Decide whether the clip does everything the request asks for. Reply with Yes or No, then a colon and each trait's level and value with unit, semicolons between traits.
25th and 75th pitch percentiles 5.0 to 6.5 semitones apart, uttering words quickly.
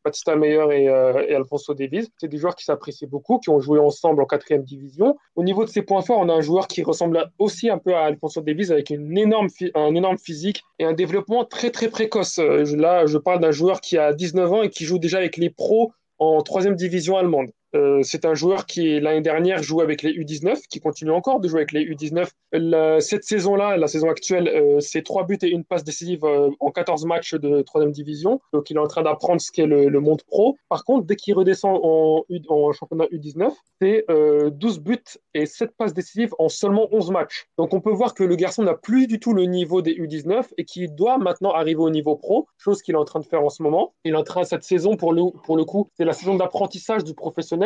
No: average, 3.9 semitones; fast, 240 wpm